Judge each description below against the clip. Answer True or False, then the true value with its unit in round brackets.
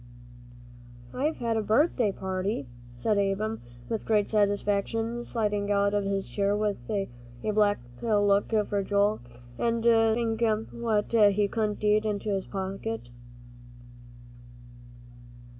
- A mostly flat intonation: True (1.8 semitones)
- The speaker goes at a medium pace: False (115 wpm)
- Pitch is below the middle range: False (210 Hz)